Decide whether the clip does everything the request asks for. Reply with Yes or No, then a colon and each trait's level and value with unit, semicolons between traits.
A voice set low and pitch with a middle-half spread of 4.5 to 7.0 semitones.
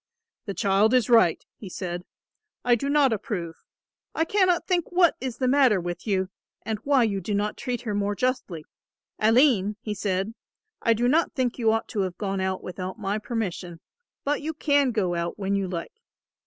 No: high, 215 Hz; average, 5.1 semitones